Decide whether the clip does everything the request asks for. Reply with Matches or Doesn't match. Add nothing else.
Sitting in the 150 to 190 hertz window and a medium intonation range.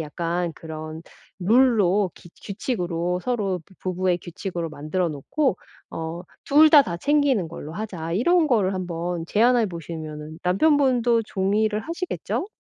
Doesn't match